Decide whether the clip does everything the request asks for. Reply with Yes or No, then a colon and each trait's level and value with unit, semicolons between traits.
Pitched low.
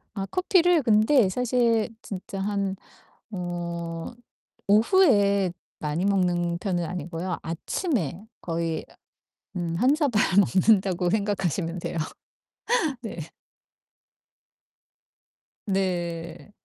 No: high, 190 Hz